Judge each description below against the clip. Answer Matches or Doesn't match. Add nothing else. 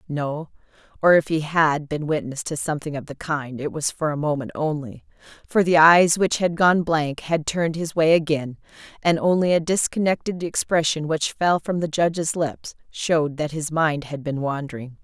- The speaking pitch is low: Doesn't match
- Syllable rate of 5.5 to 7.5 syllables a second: Doesn't match